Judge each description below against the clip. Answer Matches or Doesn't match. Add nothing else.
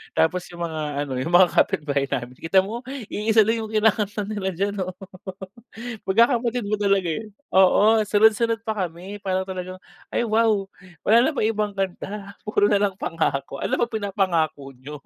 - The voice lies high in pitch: Matches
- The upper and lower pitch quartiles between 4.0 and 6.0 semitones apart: Doesn't match